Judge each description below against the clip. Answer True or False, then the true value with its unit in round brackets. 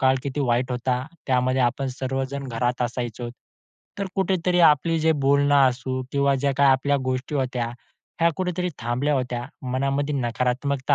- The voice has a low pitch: True (130 Hz)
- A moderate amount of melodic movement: False (2.2 semitones)